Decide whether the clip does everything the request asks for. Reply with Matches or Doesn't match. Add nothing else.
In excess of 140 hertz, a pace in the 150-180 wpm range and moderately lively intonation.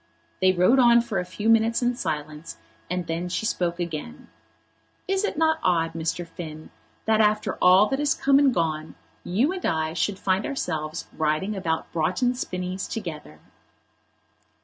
Doesn't match